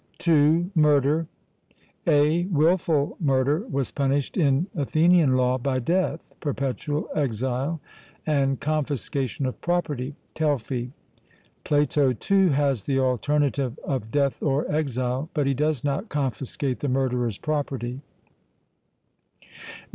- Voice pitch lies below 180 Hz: Yes, medium, 140 Hz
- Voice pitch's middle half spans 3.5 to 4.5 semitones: No, average, 2.8 semitones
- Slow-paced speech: Yes, slow, 110 wpm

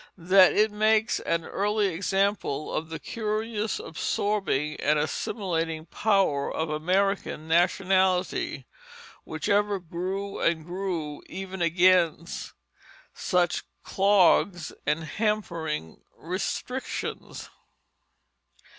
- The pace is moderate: No, slow, 90 wpm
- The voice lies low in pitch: No, medium, 185 Hz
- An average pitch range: Yes, average, 3.7 semitones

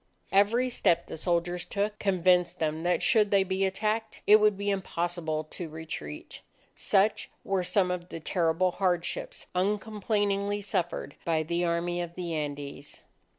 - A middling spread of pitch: Yes, average, 3.0 semitones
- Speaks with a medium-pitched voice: Yes, medium, 180 Hz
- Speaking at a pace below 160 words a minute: Yes, average, 150 wpm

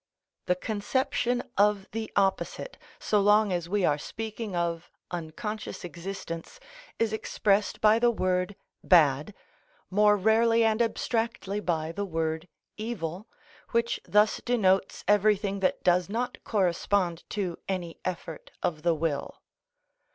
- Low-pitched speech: No, high, 200 Hz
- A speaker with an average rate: No, slow, 125 wpm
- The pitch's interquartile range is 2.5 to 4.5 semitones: Yes, average, 3.8 semitones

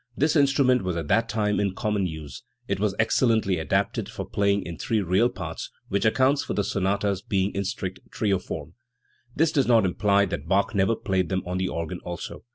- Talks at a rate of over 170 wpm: Yes, average, 200 wpm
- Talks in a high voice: No, low, 100 Hz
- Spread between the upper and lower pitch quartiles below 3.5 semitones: Yes, average, 3.1 semitones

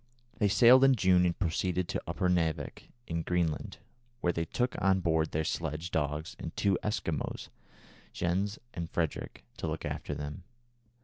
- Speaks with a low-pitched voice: Yes, very low, 85 Hz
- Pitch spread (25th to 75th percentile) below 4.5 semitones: Yes, average, 2.9 semitones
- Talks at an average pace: Yes, average, 150 wpm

